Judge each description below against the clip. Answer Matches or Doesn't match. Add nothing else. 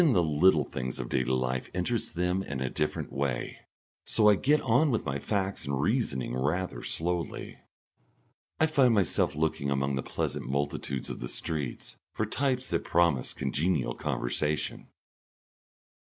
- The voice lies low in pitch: Matches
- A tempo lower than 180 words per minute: Matches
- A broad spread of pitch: Matches